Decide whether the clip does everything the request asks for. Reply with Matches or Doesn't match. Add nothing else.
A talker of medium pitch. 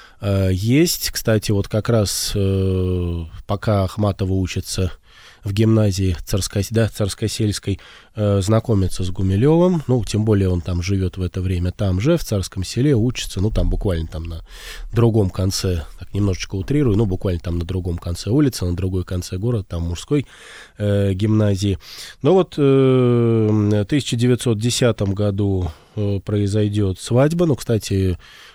Doesn't match